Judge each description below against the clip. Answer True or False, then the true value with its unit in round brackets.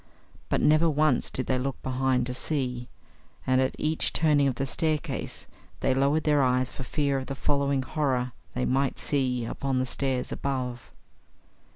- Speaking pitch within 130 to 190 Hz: True (135 Hz)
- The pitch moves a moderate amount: False (2.0 semitones)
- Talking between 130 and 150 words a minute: False (170 wpm)